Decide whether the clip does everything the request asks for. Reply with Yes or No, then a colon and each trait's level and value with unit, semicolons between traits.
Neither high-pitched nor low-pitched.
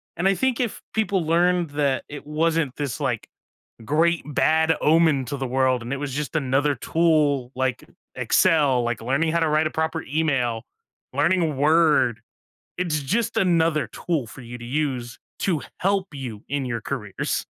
Yes: medium, 150 Hz